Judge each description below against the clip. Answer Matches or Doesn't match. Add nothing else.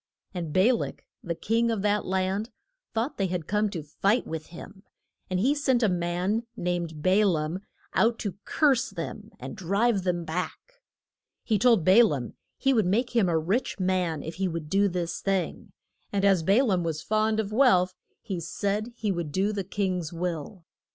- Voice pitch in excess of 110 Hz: Matches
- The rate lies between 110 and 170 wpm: Doesn't match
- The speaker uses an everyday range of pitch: Matches